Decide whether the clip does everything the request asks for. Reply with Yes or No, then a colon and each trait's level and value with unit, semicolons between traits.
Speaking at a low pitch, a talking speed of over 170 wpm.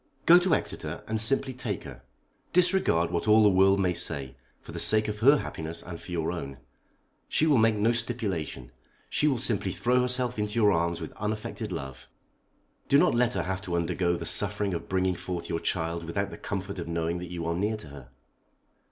Yes: very low, 95 Hz; fast, 205 wpm